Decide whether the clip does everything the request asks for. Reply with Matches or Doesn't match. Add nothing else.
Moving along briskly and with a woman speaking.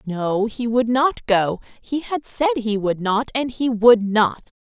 Doesn't match